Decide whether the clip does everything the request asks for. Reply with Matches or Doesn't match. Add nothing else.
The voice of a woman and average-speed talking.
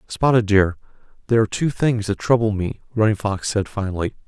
Doesn't match